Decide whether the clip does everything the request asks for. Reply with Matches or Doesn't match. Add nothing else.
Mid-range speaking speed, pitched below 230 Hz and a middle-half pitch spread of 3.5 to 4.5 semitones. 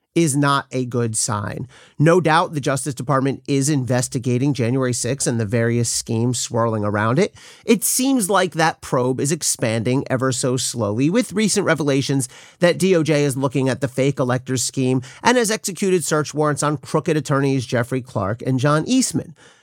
Matches